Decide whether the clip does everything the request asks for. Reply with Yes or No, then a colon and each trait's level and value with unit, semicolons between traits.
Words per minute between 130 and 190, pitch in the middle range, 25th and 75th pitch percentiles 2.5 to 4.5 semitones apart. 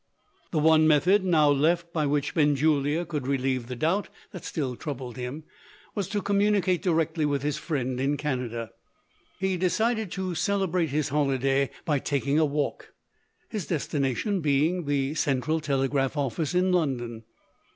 Yes: average, 150 wpm; medium, 150 Hz; average, 4.1 semitones